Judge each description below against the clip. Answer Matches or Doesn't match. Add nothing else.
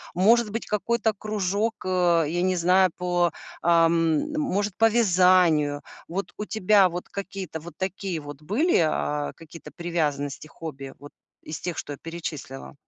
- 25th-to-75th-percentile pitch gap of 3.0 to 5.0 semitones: Matches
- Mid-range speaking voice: Matches